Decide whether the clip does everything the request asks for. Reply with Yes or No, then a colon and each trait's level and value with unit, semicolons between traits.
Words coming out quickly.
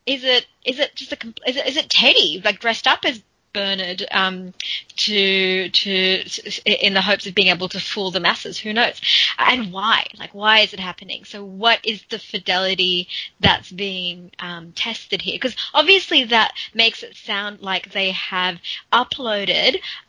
No: average, 175 wpm